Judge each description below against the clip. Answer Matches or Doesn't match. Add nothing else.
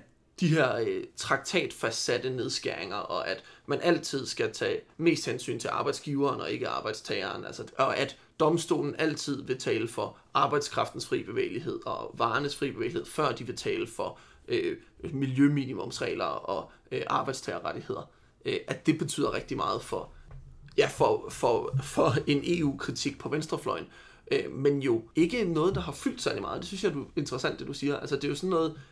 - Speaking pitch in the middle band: Matches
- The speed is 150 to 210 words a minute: Matches